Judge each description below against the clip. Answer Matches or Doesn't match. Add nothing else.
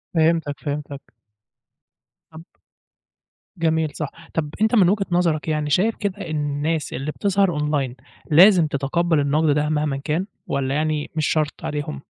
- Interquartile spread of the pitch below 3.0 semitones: Matches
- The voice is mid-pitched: Matches